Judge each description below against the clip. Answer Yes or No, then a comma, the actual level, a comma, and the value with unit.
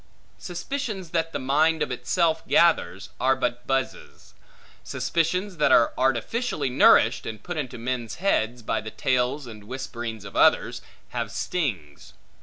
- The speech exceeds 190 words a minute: No, average, 145 wpm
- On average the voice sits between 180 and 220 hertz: No, low, 130 Hz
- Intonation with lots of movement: Yes, wide, 5.8 semitones